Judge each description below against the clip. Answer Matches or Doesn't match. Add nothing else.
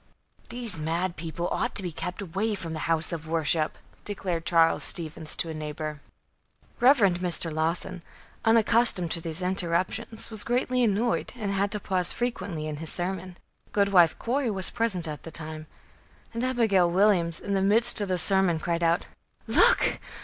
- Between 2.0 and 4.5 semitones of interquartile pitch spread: Matches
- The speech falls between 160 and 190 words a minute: Matches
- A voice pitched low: Doesn't match